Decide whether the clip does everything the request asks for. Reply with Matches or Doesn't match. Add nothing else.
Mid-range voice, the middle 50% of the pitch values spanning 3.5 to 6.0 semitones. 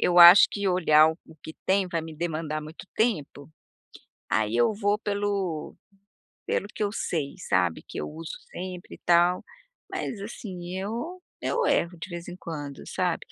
Matches